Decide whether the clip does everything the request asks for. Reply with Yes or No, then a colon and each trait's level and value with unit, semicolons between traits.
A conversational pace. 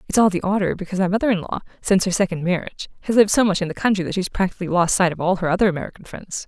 No: fast, 285 wpm